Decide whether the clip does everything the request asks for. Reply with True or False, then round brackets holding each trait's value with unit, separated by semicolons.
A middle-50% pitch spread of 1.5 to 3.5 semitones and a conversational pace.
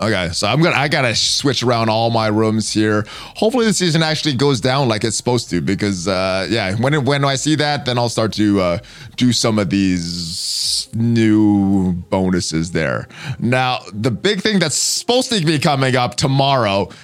False (5.6 semitones; 185 wpm)